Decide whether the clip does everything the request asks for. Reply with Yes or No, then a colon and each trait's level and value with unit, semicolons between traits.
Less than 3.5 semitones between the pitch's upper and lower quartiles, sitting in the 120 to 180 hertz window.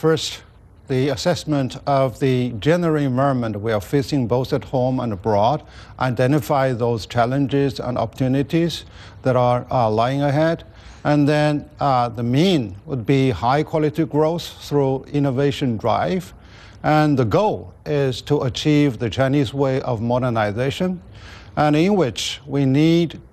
No: average, 3.9 semitones; low, 135 Hz